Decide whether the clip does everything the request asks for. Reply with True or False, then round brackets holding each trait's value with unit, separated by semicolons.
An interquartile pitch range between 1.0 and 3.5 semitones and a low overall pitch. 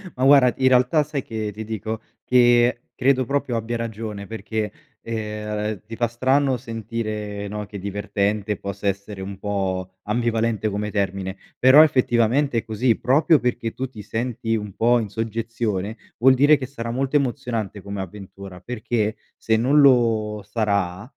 True (2.9 semitones; 110 Hz)